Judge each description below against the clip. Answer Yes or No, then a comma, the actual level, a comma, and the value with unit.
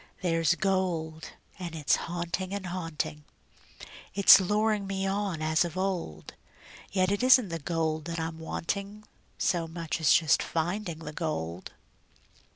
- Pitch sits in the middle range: Yes, medium, 170 Hz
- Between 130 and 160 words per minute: Yes, average, 140 wpm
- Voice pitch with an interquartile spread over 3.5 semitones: No, average, 3.2 semitones